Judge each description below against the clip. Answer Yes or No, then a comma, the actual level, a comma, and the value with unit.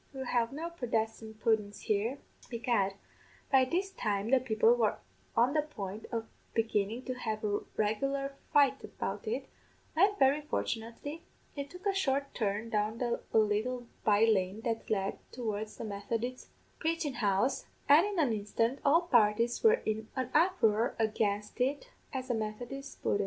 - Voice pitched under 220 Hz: No, high, 235 Hz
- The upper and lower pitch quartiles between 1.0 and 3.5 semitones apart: No, average, 4.5 semitones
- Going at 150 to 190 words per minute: Yes, average, 155 wpm